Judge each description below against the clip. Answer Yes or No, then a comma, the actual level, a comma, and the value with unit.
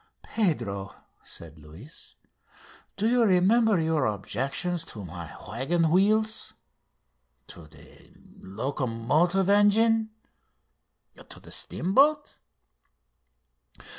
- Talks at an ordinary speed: No, slow, 80 wpm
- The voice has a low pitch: No, medium, 165 Hz